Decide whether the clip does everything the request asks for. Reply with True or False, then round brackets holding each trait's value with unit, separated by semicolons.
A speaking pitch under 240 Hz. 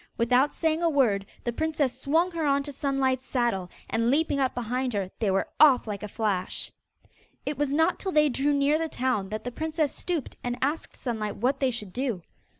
False (260 Hz)